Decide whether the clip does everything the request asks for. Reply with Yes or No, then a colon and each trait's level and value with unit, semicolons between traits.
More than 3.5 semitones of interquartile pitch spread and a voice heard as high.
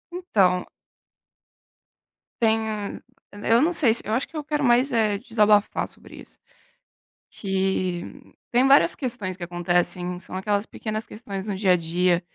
Yes: average, 4.6 semitones; high, 210 Hz